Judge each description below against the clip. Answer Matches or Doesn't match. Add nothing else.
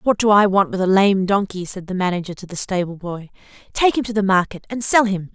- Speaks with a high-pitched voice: Matches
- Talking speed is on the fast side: Matches